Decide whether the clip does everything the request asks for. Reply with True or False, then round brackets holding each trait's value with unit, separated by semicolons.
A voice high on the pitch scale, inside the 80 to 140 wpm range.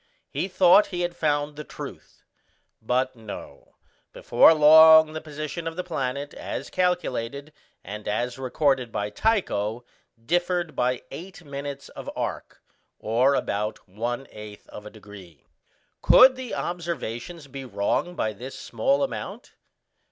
False (140 Hz; 135 wpm)